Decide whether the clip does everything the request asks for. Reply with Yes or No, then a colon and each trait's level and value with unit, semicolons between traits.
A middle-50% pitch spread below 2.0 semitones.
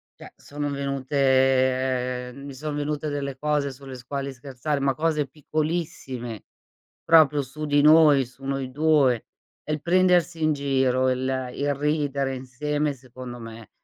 No: narrow, 2.4 semitones